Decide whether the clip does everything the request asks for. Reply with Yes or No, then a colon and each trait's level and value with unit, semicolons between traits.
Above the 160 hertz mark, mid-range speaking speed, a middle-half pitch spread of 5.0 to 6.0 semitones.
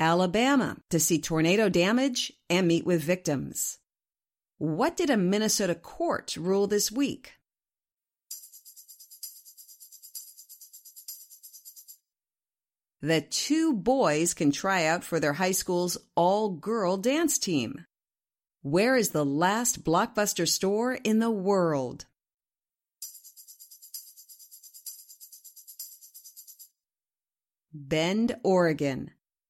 No: medium, 185 Hz; slow, 85 wpm; wide, 5.6 semitones